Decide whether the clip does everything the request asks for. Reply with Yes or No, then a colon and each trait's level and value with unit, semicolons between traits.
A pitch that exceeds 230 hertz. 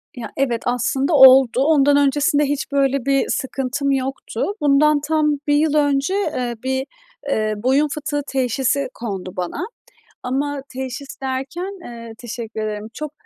Yes: very high, 270 Hz